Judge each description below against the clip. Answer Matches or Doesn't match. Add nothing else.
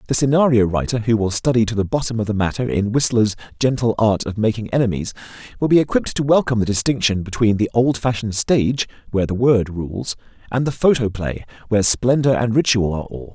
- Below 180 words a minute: Doesn't match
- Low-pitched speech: Matches